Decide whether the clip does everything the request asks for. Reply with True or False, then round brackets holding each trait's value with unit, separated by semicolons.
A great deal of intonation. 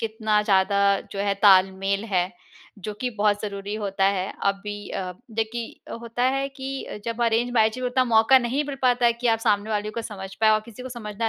False (3.0 semitones)